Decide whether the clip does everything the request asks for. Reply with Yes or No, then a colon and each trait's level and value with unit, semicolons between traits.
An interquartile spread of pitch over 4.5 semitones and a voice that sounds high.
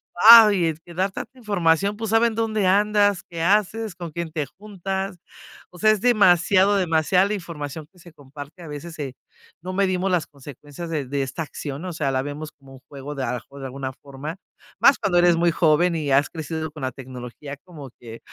No: average, 5.1 semitones; medium, 165 Hz